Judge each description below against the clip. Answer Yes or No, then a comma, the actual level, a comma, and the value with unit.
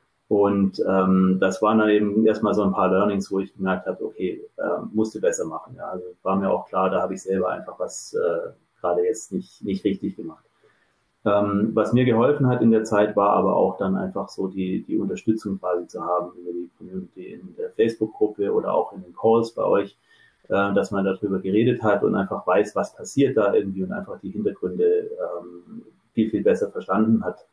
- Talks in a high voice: No, low, 110 Hz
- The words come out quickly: Yes, fast, 205 wpm